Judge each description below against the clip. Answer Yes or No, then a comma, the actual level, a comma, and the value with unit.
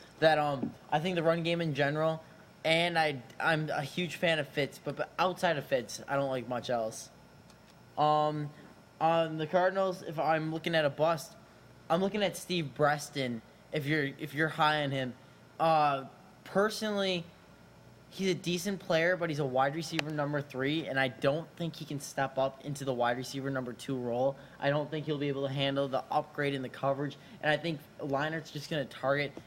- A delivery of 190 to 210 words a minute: Yes, average, 200 wpm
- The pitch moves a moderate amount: Yes, average, 3.0 semitones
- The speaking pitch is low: No, medium, 150 Hz